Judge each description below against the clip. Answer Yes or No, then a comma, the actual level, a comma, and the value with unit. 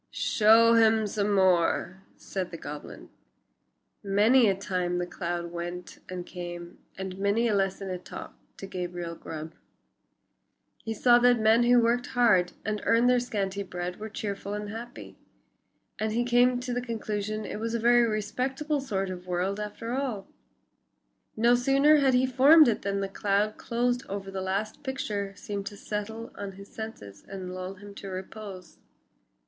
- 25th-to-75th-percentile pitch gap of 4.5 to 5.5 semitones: No, average, 3.8 semitones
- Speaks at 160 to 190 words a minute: Yes, average, 165 wpm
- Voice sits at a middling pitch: No, high, 205 Hz